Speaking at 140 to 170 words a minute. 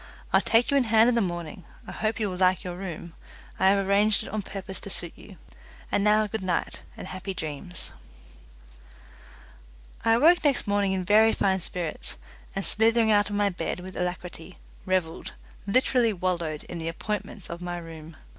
No: average, 185 wpm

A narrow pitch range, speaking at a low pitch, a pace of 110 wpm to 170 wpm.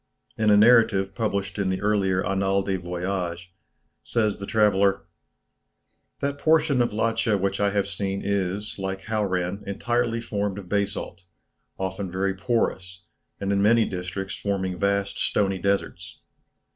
Yes: narrow, 1.9 semitones; low, 100 Hz; average, 140 wpm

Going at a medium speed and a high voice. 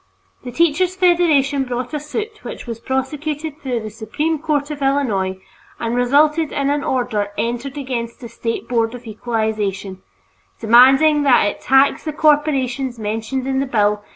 Yes: average, 155 wpm; very high, 265 Hz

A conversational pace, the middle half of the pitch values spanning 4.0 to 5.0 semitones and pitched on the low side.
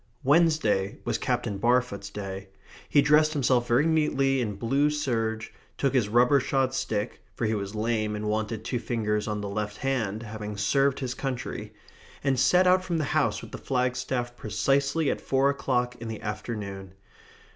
Yes: average, 170 wpm; average, 4.4 semitones; low, 120 Hz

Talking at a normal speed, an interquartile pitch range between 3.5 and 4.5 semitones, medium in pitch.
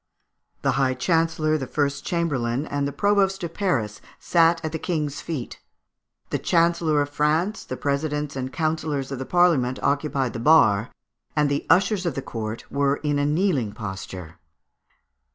Yes: average, 160 wpm; average, 4.0 semitones; medium, 145 Hz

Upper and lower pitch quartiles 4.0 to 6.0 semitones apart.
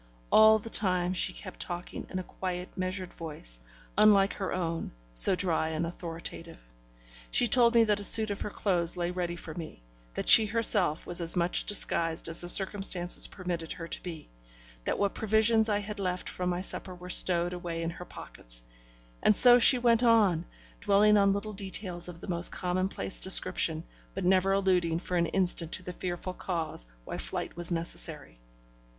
No: average, 3.0 semitones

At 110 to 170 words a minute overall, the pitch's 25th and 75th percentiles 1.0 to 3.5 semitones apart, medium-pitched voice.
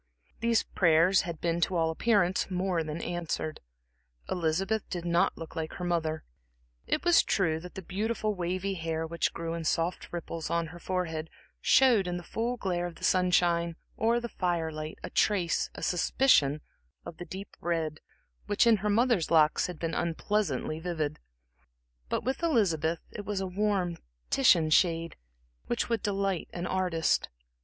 Yes: average, 165 wpm; average, 3.2 semitones; medium, 175 Hz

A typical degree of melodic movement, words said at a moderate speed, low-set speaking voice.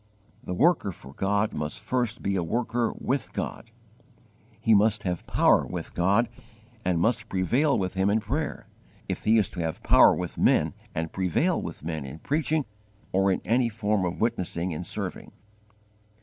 Yes: average, 4.7 semitones; average, 170 wpm; low, 100 Hz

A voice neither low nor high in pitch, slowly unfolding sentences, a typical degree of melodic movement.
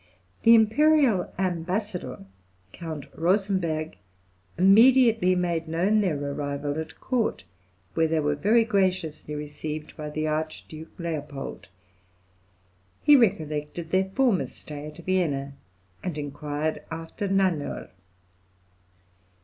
Yes: medium, 165 Hz; slow, 100 wpm; average, 4.5 semitones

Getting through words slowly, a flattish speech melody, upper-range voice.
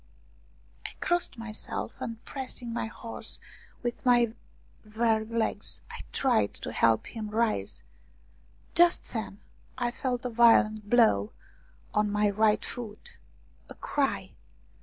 Yes: slow, 120 wpm; narrow, 2.2 semitones; high, 230 Hz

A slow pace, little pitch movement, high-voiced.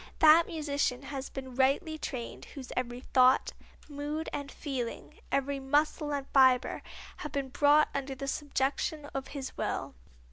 No: average, 145 wpm; narrow, 2.0 semitones; very high, 275 Hz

